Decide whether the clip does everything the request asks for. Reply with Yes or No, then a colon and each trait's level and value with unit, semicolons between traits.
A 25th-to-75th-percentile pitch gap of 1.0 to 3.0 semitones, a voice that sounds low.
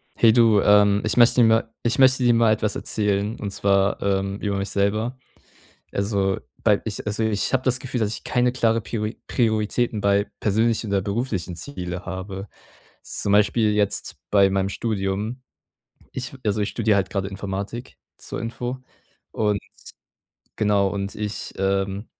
Yes: narrow, 2.6 semitones; low, 105 Hz